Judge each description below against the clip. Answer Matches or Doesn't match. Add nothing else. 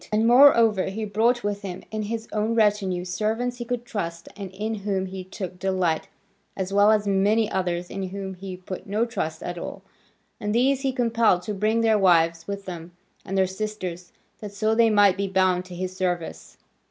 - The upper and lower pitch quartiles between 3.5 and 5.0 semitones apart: Doesn't match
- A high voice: Matches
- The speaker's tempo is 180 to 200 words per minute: Matches